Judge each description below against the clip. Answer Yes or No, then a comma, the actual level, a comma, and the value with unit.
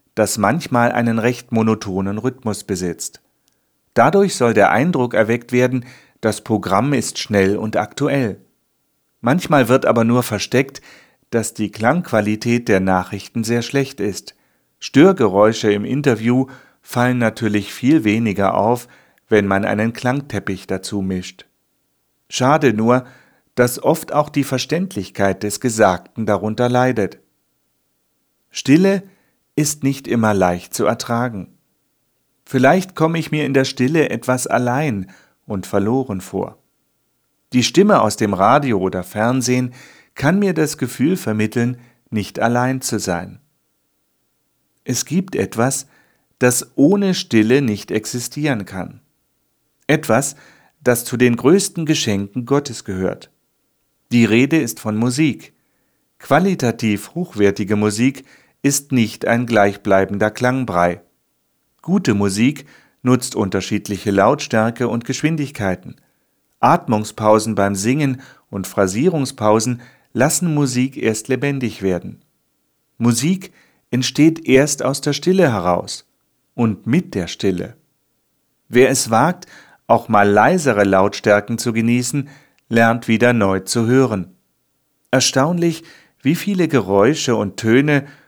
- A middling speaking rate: No, slow, 115 wpm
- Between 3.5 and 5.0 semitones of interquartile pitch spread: Yes, average, 4.4 semitones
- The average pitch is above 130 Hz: No, low, 120 Hz